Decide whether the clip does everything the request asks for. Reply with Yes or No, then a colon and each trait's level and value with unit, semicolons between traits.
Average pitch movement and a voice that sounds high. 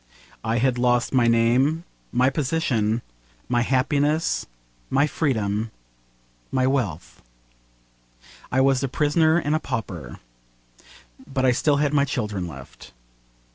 No: average, 3.9 semitones; low, 130 Hz